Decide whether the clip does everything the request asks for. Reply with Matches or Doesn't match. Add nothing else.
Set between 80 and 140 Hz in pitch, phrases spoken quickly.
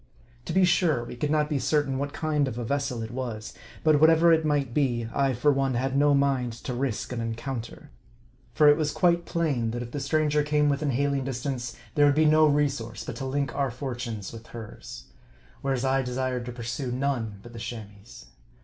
Matches